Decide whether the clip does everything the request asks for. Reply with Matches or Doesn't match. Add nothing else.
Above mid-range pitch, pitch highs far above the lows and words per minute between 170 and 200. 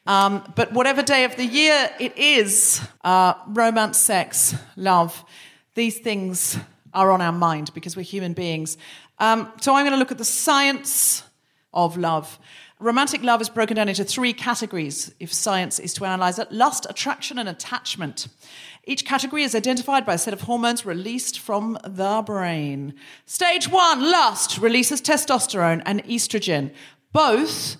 Doesn't match